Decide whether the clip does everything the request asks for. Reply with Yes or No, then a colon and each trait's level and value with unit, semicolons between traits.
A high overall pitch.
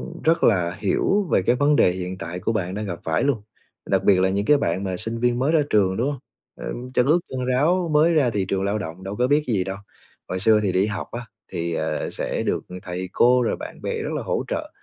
No: low, 105 Hz